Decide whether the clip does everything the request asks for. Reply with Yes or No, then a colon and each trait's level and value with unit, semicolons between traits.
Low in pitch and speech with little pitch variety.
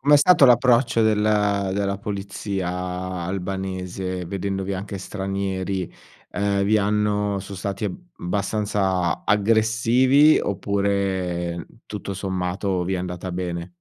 Yes: low, 100 Hz; narrow, 2.0 semitones